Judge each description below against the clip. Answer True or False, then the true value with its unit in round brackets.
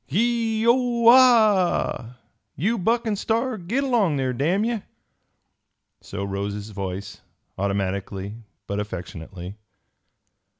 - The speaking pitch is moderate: True (175 Hz)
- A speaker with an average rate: False (110 wpm)